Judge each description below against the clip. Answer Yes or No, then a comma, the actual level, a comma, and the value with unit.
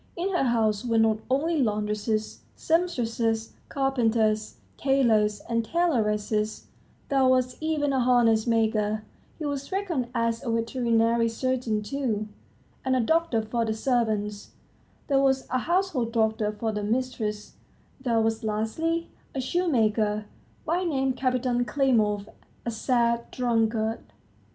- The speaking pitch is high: Yes, high, 235 Hz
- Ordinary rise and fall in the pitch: Yes, average, 3.6 semitones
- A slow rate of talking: Yes, slow, 125 wpm